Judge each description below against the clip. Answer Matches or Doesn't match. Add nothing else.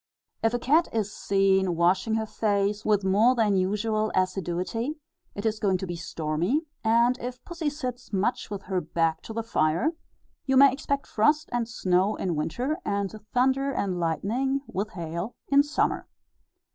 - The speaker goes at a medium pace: Matches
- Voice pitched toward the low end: Doesn't match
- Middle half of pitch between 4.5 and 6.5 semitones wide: Matches